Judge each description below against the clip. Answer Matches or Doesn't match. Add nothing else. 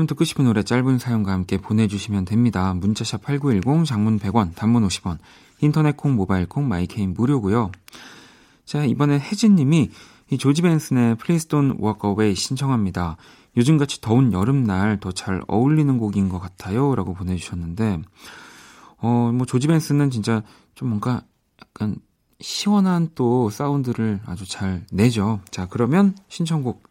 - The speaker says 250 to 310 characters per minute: Matches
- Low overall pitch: Matches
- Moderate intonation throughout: Doesn't match